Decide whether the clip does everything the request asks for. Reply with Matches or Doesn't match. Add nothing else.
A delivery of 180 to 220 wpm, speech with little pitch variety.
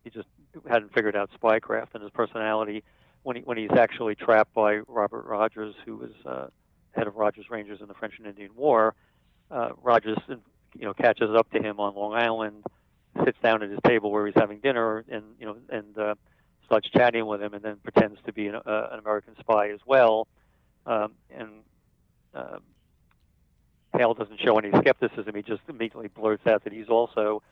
Matches